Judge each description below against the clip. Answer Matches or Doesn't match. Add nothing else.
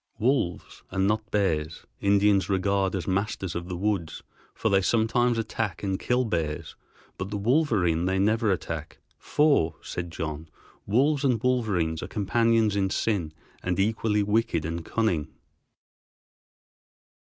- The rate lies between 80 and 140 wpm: Matches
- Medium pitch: Doesn't match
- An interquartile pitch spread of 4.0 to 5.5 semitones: Matches